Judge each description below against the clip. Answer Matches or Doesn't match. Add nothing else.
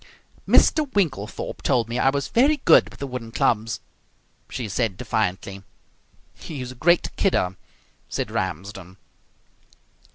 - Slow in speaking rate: Matches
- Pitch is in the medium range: Doesn't match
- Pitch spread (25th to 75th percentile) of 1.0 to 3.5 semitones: Doesn't match